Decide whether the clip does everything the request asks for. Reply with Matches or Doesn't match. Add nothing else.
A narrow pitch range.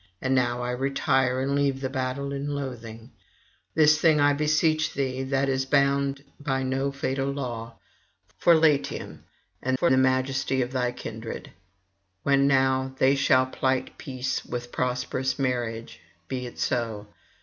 Matches